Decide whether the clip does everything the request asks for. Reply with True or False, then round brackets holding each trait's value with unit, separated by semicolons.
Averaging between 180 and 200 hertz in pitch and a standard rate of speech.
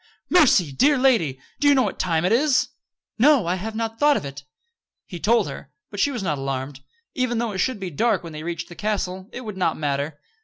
False (190 Hz; 230 wpm)